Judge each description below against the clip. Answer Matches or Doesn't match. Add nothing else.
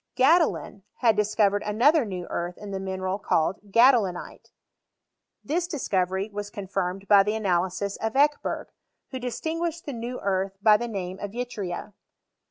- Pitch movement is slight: Doesn't match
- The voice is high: Matches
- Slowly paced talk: Doesn't match